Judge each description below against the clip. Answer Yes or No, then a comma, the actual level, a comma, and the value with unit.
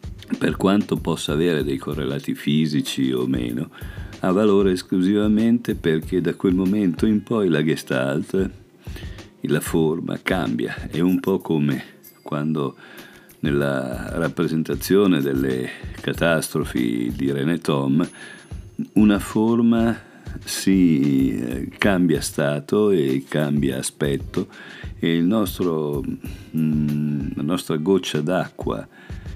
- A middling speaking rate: No, slow, 100 wpm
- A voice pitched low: Yes, very low, 80 Hz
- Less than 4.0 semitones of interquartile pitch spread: No, average, 5.1 semitones